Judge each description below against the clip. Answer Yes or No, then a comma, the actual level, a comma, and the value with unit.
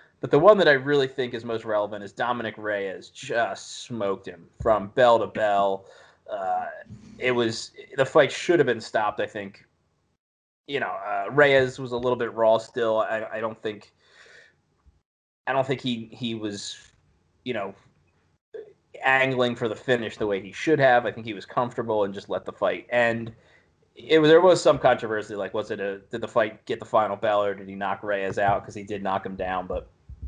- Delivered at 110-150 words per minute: No, average, 200 wpm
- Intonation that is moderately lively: Yes, average, 4.5 semitones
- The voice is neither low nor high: No, low, 115 Hz